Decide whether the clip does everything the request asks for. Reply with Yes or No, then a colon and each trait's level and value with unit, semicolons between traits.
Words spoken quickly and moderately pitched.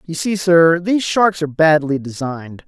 No: average, 180 wpm; medium, 165 Hz